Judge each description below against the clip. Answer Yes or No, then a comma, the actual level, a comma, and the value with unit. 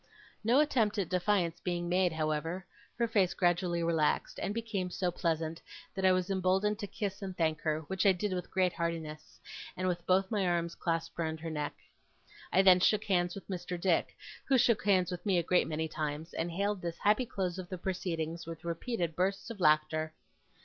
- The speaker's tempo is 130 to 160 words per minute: No, average, 200 wpm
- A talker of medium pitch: Yes, medium, 180 Hz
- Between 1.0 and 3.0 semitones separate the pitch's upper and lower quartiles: Yes, average, 2.7 semitones